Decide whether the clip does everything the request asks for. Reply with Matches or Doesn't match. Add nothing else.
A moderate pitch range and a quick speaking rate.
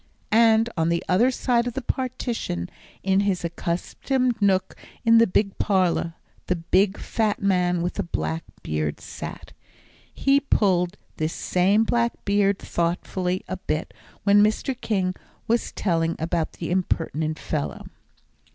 Doesn't match